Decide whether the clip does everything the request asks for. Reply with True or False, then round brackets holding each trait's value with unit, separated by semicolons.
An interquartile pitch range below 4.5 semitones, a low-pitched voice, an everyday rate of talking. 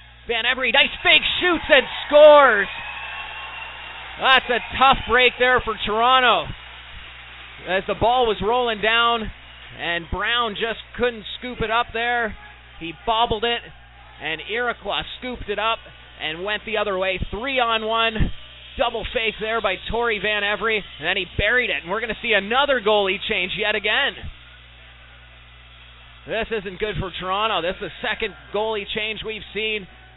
False (4.0 semitones; 215 Hz; 155 wpm)